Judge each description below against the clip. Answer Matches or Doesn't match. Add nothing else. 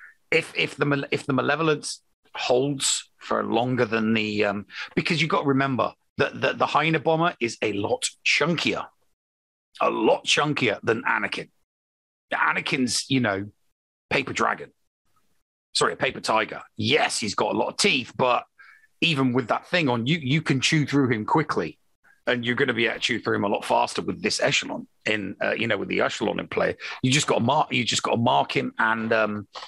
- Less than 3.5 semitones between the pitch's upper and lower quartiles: Doesn't match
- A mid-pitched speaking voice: Doesn't match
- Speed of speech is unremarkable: Matches